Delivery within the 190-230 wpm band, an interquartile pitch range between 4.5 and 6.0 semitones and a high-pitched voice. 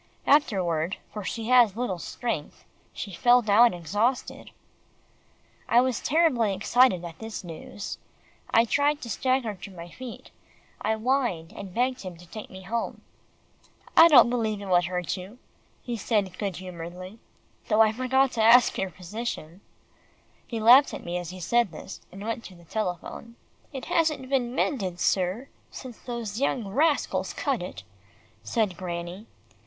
No: average, 155 wpm; average, 5.1 semitones; high, 220 Hz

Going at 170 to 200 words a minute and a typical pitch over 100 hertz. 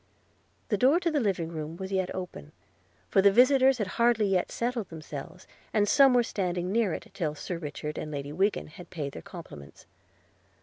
Yes: average, 180 wpm; high, 190 Hz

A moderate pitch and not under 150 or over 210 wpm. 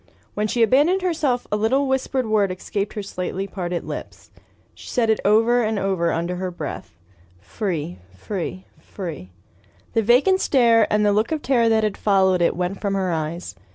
No: high, 205 Hz; average, 180 wpm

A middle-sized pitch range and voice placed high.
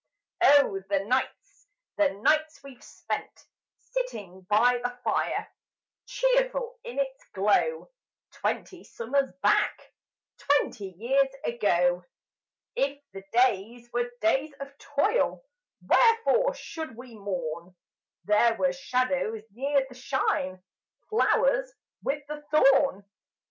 No: wide, 6.2 semitones; very high, 265 Hz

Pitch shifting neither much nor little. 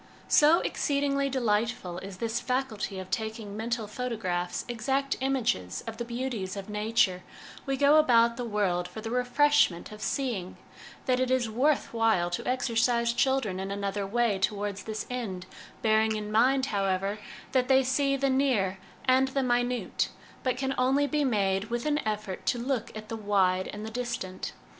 Yes: average, 4.2 semitones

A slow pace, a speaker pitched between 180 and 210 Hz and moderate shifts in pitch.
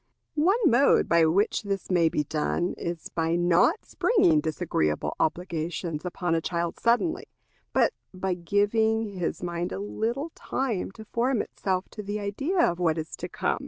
No: average, 160 wpm; medium, 185 Hz; average, 4.9 semitones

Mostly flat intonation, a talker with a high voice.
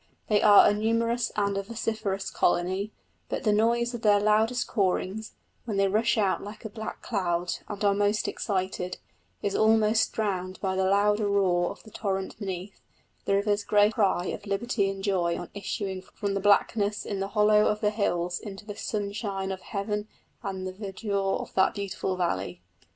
Yes: narrow, 1.8 semitones; high, 200 Hz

